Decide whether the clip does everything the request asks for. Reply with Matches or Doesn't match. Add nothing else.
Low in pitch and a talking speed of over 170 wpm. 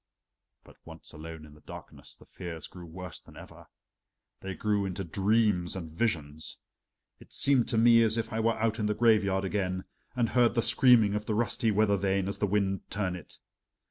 Matches